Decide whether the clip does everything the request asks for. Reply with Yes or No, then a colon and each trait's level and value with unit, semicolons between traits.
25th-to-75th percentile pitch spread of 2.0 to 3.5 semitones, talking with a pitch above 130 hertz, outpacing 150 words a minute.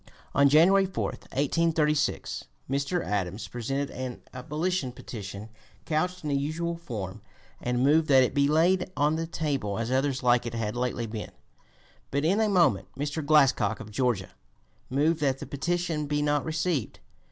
No: average, 4.6 semitones; medium, 140 Hz; average, 160 wpm